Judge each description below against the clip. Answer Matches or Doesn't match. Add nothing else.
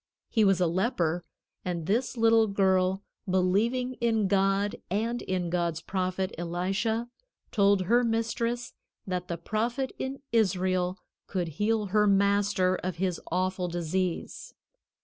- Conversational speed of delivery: Doesn't match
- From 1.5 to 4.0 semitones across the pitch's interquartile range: Matches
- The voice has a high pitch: Matches